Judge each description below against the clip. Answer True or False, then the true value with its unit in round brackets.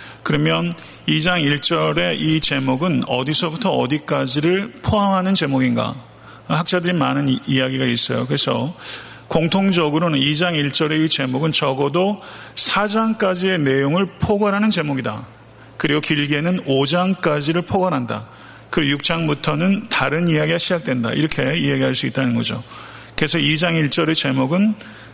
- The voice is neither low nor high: True (155 Hz)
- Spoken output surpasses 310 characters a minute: False (300 characters per minute)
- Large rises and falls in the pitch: False (4.8 semitones)